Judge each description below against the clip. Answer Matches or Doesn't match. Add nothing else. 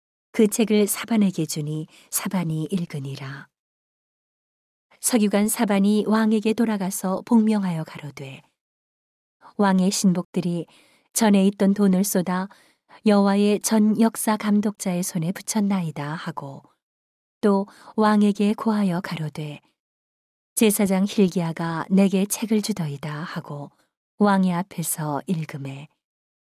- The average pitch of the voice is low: Doesn't match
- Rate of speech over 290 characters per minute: Doesn't match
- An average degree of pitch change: Matches